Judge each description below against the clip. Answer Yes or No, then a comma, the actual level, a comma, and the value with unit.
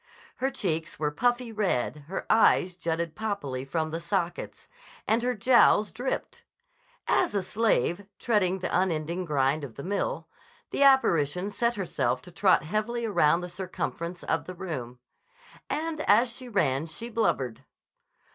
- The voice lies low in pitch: No, medium, 185 Hz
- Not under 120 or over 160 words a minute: Yes, average, 145 wpm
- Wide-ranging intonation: Yes, wide, 5.8 semitones